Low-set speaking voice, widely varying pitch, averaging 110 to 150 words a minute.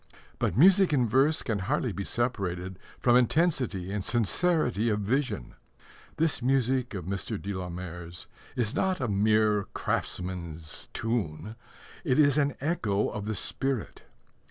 Yes: low, 110 Hz; wide, 5.7 semitones; average, 140 wpm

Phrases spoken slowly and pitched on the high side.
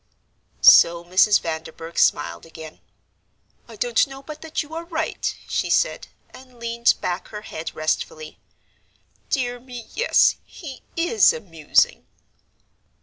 Yes: slow, 125 wpm; high, 235 Hz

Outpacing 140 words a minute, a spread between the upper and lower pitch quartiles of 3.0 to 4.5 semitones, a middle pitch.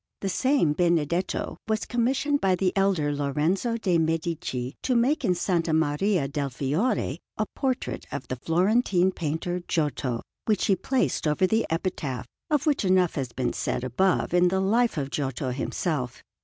No: average, 160 wpm; wide, 5.6 semitones; medium, 175 Hz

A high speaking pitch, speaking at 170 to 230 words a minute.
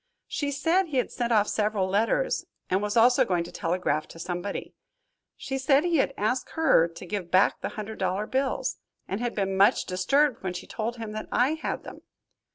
Yes: high, 215 Hz; average, 200 wpm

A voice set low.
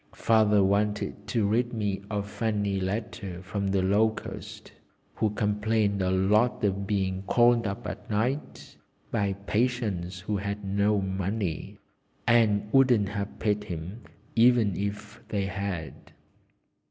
Yes: low, 105 Hz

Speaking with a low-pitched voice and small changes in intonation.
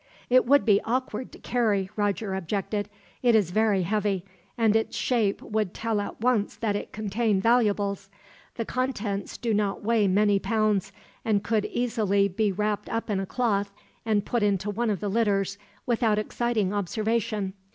No: high, 210 Hz; narrow, 2.3 semitones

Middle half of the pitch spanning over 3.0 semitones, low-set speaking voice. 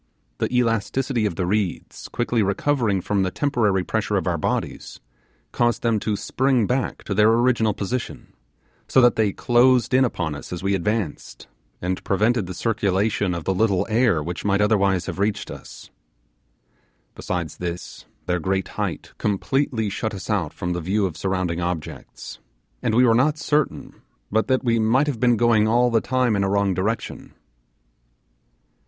Yes: average, 4.1 semitones; low, 105 Hz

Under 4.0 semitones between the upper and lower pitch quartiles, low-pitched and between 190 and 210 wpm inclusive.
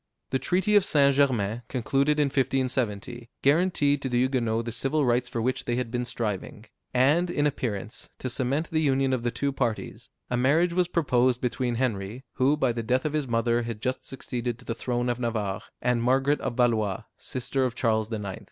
Yes: average, 2.9 semitones; low, 125 Hz; average, 200 wpm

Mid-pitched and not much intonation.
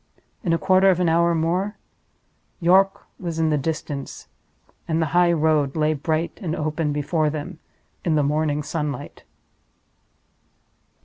Yes: medium, 160 Hz; narrow, 2.1 semitones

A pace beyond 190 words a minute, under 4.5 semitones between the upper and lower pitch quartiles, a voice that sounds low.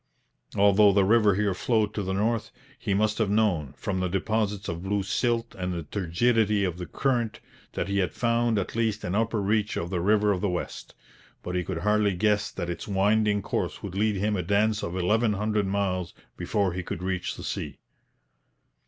Yes: average, 200 wpm; narrow, 2.5 semitones; low, 100 Hz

